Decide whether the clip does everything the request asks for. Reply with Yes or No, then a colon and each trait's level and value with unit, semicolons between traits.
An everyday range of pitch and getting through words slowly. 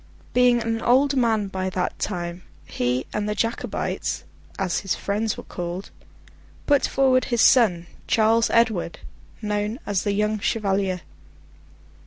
Yes: average, 3.6 semitones; slow, 125 wpm